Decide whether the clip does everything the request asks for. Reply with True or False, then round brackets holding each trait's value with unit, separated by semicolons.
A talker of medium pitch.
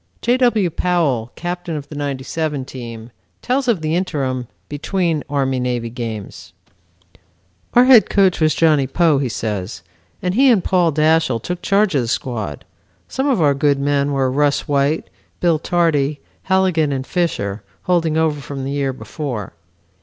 True (150 Hz)